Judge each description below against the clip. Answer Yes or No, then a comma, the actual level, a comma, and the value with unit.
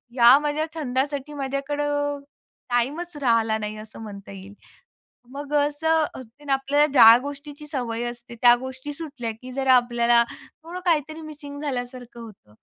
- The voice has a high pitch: Yes, very high, 270 Hz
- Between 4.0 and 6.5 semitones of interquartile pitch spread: No, average, 3.6 semitones